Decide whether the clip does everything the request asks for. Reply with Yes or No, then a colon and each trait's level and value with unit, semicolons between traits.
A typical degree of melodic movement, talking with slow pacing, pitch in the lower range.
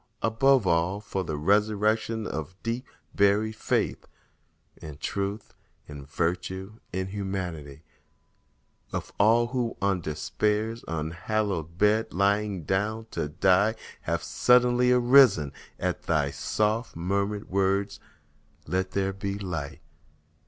Yes: average, 3.6 semitones; slow, 105 wpm; low, 100 Hz